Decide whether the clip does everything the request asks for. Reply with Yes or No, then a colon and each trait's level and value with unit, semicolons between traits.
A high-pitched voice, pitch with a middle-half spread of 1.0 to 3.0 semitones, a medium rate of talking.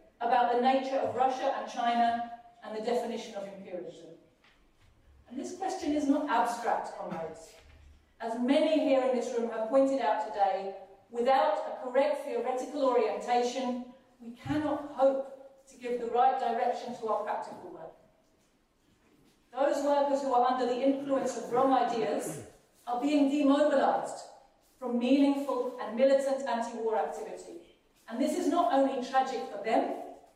Yes: very high, 250 Hz; narrow, 2.6 semitones; average, 145 wpm